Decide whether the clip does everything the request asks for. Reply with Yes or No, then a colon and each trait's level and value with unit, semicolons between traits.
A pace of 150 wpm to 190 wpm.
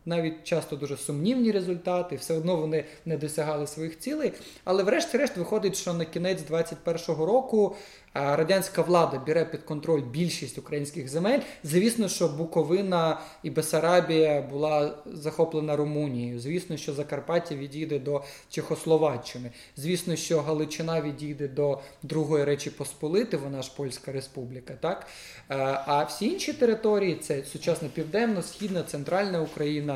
No: average, 130 wpm